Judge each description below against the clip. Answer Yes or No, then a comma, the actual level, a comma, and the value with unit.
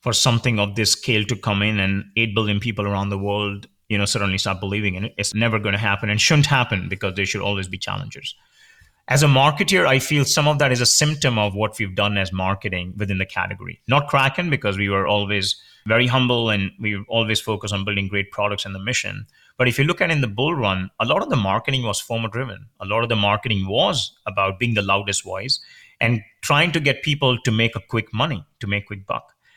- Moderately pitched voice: No, low, 110 Hz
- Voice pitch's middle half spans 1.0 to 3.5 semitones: No, average, 4.0 semitones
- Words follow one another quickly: Yes, fast, 235 wpm